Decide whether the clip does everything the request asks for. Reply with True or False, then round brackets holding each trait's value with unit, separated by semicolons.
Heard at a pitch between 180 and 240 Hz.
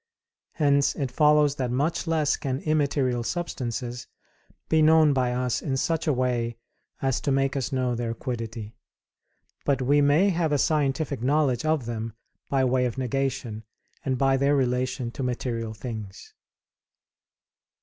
False (130 Hz)